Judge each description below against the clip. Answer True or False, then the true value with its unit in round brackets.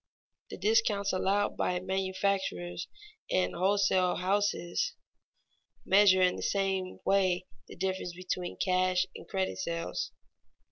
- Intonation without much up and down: True (1.4 semitones)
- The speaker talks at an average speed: False (110 wpm)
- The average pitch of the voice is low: False (190 Hz)